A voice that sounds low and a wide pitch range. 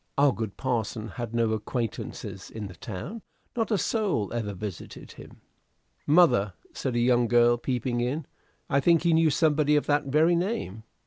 Yes: low, 125 Hz; wide, 5.7 semitones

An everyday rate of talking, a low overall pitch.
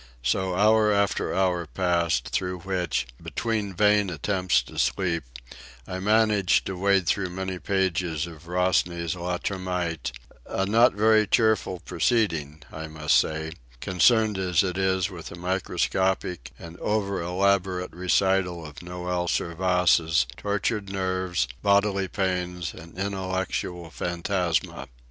No: slow, 120 wpm; very low, 90 Hz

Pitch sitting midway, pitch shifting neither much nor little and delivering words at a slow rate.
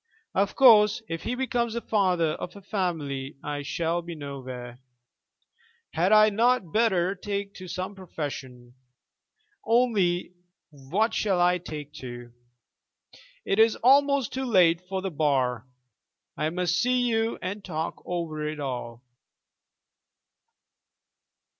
No: medium, 180 Hz; wide, 6.2 semitones; slow, 125 wpm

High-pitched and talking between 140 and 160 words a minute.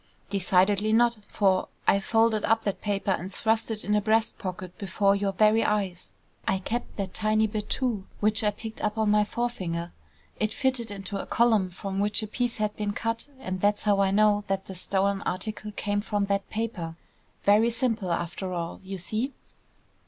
No: high, 205 Hz; average, 190 wpm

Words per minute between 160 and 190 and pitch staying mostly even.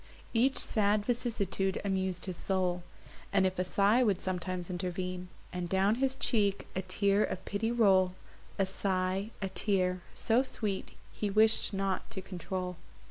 No: average, 150 wpm; narrow, 2.3 semitones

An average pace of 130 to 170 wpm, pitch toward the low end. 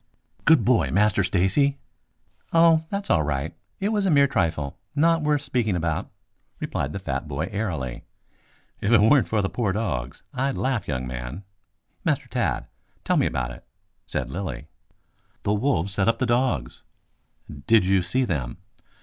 Yes: average, 160 wpm; low, 100 Hz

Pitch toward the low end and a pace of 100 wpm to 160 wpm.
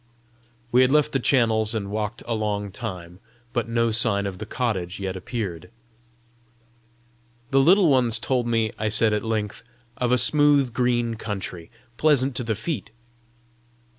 Yes: low, 115 Hz; average, 155 wpm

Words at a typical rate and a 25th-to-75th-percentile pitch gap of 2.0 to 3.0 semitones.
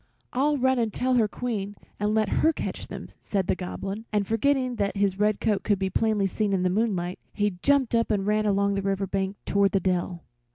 No: fast, 220 wpm; narrow, 2.6 semitones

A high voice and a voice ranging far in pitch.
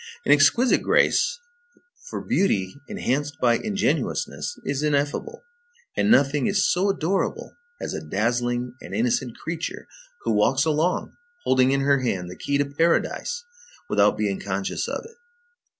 No: medium, 140 Hz; wide, 6.1 semitones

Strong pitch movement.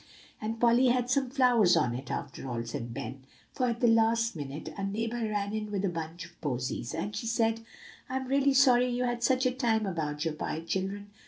Yes: wide, 6.9 semitones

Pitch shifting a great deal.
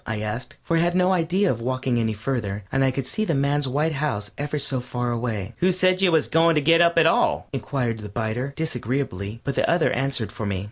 Yes: wide, 6.1 semitones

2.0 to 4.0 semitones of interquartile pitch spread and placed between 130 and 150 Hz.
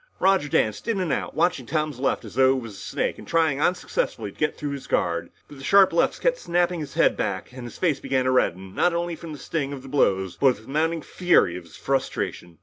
No: average, 5.1 semitones; medium, 140 Hz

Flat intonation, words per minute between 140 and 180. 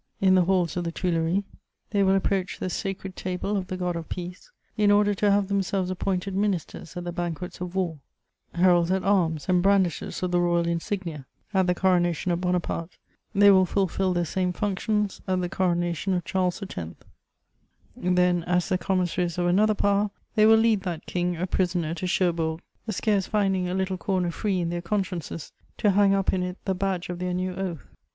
No: narrow, 1.8 semitones; average, 195 wpm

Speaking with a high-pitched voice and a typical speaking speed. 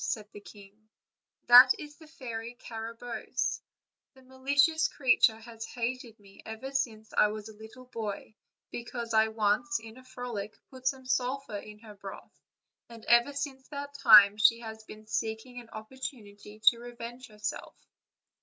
Yes: high, 230 Hz; average, 155 wpm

